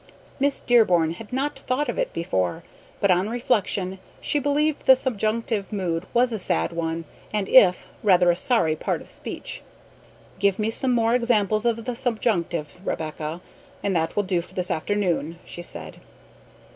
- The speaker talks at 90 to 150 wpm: No, average, 165 wpm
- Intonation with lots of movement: Yes, wide, 5.7 semitones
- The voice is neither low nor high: No, high, 200 Hz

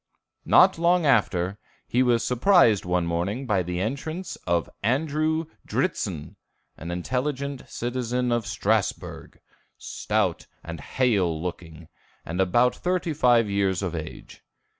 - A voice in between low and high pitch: No, low, 115 Hz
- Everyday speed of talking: No, slow, 120 wpm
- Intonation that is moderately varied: No, wide, 7.6 semitones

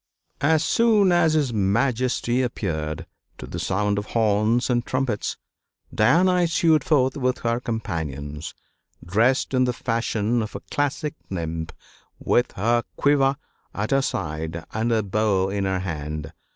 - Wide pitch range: Yes, wide, 5.7 semitones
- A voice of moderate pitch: No, low, 115 Hz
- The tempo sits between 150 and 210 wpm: No, average, 140 wpm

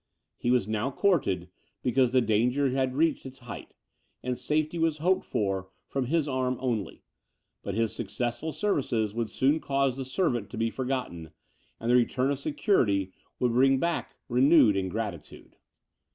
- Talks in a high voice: No, low, 125 Hz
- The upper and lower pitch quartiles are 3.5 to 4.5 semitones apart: Yes, average, 3.8 semitones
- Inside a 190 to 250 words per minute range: No, average, 155 wpm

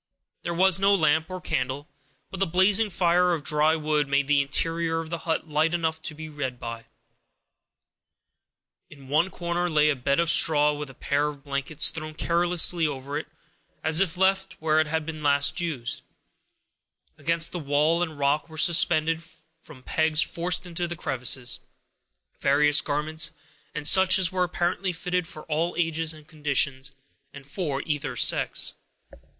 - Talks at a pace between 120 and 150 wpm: No, average, 165 wpm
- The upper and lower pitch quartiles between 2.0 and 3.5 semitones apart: Yes, average, 2.8 semitones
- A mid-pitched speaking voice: Yes, medium, 155 Hz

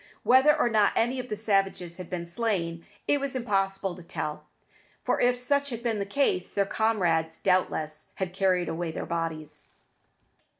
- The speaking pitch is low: No, high, 195 Hz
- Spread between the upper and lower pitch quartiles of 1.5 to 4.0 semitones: No, wide, 5.6 semitones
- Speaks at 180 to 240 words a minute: No, average, 170 wpm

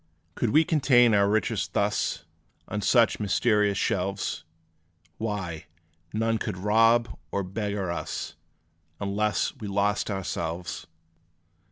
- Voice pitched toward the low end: Yes, low, 105 Hz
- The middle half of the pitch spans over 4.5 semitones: No, narrow, 2.5 semitones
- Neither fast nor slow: No, slow, 110 wpm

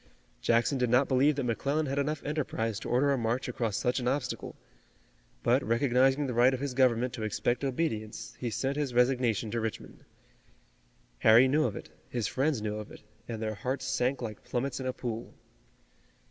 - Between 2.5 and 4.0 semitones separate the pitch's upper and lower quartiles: Yes, average, 2.8 semitones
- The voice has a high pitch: No, low, 125 Hz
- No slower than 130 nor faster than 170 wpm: No, average, 190 wpm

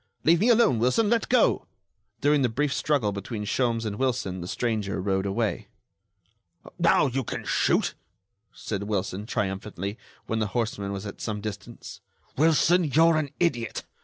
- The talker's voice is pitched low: Yes, low, 115 Hz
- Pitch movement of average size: No, wide, 6.4 semitones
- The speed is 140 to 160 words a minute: Yes, average, 155 wpm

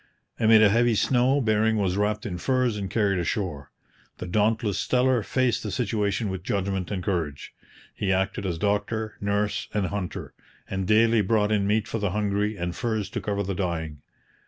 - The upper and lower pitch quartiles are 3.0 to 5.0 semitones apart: No, narrow, 2.6 semitones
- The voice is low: Yes, low, 105 Hz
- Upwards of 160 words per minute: Yes, average, 180 wpm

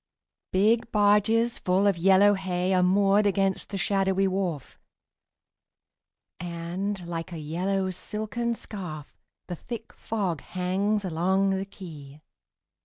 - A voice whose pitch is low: No, high, 190 Hz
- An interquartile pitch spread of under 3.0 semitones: Yes, narrow, 2.5 semitones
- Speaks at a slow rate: Yes, slow, 115 wpm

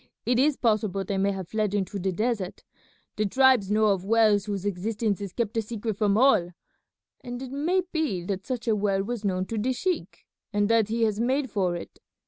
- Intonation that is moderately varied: Yes, average, 3.3 semitones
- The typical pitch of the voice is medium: No, high, 215 Hz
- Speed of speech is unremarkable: No, fast, 210 wpm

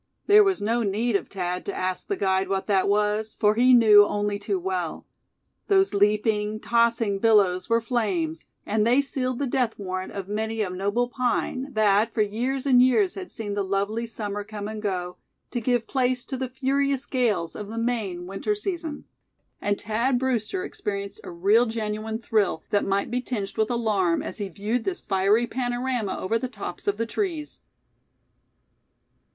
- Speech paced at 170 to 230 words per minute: Yes, average, 180 wpm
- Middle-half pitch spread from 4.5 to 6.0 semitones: No, average, 3.7 semitones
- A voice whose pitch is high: Yes, high, 220 Hz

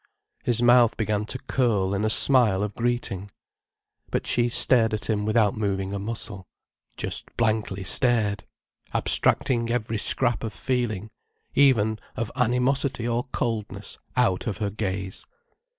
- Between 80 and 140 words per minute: Yes, slow, 135 wpm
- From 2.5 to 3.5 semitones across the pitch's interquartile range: Yes, average, 3.0 semitones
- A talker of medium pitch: No, low, 110 Hz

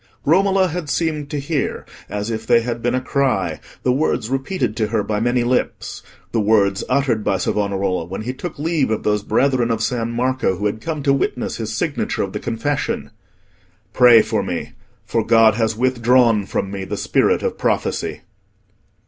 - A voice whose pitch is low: Yes, low, 120 Hz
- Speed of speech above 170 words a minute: Yes, average, 180 wpm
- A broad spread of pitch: No, average, 4.1 semitones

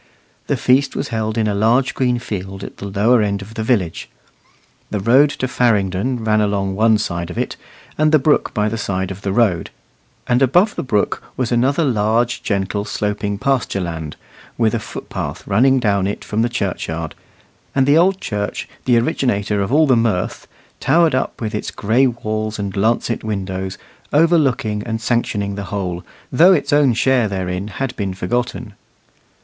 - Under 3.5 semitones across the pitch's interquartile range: No, average, 4.0 semitones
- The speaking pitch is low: Yes, low, 110 Hz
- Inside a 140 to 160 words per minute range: No, average, 175 wpm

